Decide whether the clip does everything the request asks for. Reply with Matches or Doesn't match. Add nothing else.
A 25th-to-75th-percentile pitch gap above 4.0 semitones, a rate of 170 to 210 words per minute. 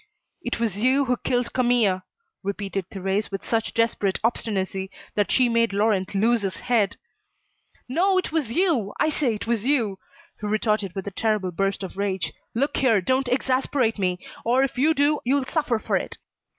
Matches